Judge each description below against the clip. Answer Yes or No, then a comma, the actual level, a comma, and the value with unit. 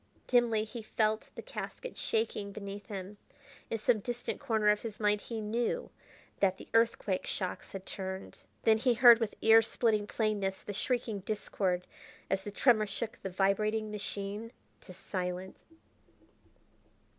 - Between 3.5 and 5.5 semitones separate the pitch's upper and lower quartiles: No, narrow, 2.4 semitones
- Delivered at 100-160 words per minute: Yes, average, 145 wpm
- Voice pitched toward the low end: No, high, 215 Hz